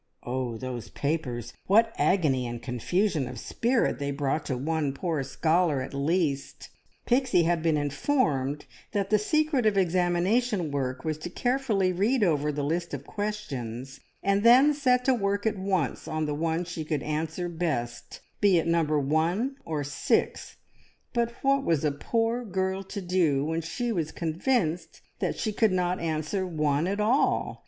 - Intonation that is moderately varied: No, wide, 6.0 semitones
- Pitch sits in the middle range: Yes, medium, 170 Hz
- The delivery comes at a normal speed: Yes, average, 165 wpm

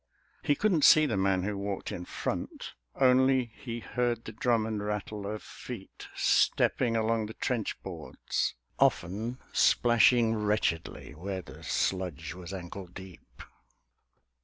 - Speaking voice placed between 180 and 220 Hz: No, low, 105 Hz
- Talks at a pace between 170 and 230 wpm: No, slow, 135 wpm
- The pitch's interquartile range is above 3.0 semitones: Yes, average, 3.8 semitones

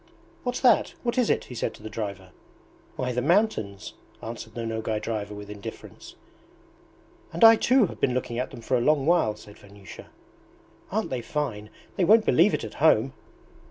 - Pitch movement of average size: No, wide, 8.6 semitones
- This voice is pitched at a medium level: No, low, 120 Hz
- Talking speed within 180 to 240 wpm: Yes, average, 185 wpm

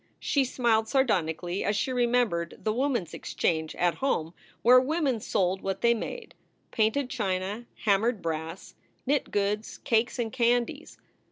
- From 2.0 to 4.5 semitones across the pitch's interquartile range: No, average, 4.9 semitones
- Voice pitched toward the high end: Yes, high, 220 Hz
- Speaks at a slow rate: No, average, 145 wpm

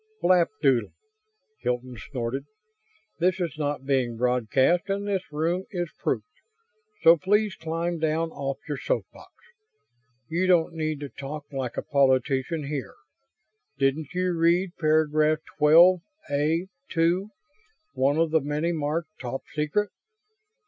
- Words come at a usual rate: No, slow, 125 wpm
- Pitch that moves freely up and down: No, average, 3.8 semitones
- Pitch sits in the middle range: Yes, medium, 155 Hz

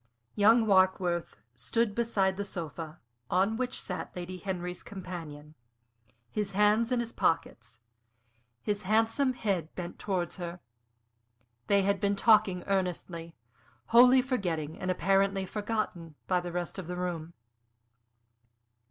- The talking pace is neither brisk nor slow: No, slow, 125 wpm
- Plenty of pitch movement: No, average, 3.2 semitones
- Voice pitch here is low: No, high, 190 Hz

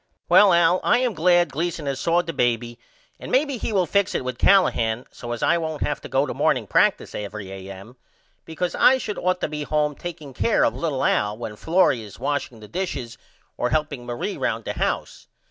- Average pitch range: No, wide, 6.5 semitones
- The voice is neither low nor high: Yes, medium, 150 Hz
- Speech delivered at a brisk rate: Yes, fast, 210 wpm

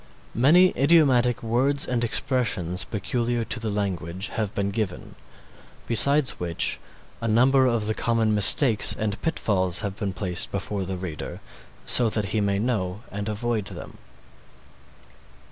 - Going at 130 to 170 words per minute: Yes, average, 140 wpm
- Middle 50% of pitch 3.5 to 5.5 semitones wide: Yes, average, 3.8 semitones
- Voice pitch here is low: Yes, low, 110 Hz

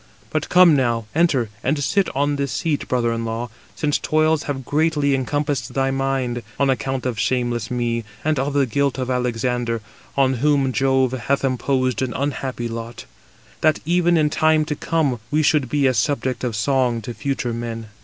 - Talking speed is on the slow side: No, average, 180 wpm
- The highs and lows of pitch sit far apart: No, average, 3.2 semitones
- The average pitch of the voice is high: No, low, 135 Hz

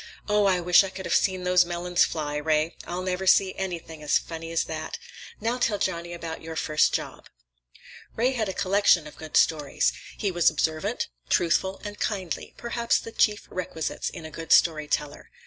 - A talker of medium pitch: Yes, medium, 175 Hz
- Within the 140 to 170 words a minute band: No, average, 180 wpm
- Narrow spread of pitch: No, average, 3.2 semitones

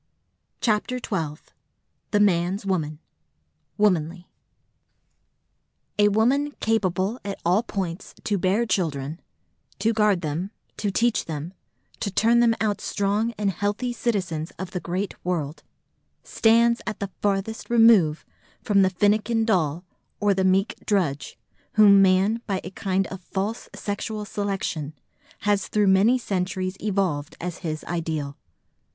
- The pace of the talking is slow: Yes, slow, 130 wpm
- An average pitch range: Yes, average, 3.2 semitones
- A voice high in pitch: Yes, high, 195 Hz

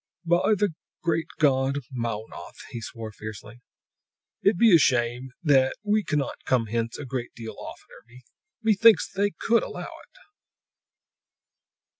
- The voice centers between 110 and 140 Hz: Yes, low, 135 Hz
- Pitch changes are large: Yes, wide, 7.6 semitones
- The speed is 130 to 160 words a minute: Yes, slow, 135 wpm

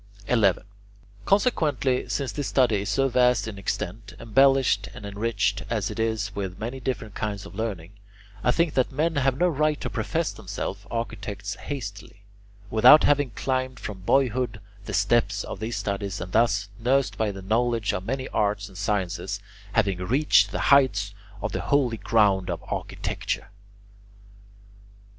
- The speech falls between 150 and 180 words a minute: Yes, average, 155 wpm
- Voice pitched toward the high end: No, low, 110 Hz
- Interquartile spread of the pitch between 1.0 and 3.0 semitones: No, average, 4.5 semitones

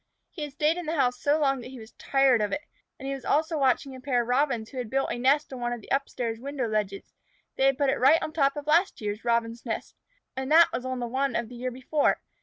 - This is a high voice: Yes, very high, 265 Hz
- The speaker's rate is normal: No, fast, 280 wpm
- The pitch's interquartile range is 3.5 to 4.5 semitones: No, average, 3.0 semitones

